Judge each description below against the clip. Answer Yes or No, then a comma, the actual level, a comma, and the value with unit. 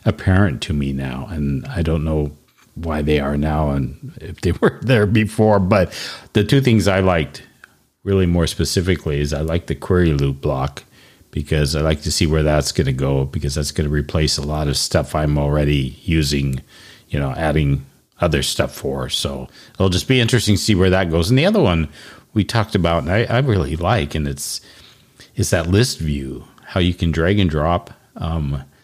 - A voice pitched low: Yes, very low, 80 Hz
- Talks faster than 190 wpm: Yes, average, 200 wpm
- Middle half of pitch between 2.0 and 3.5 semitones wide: No, wide, 5.4 semitones